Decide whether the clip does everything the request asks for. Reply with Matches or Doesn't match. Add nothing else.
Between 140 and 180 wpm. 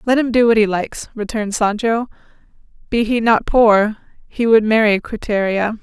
Matches